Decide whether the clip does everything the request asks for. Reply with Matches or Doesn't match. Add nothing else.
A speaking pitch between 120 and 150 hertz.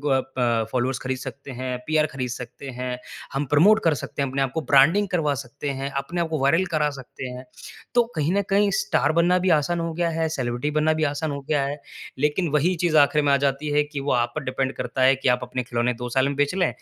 Matches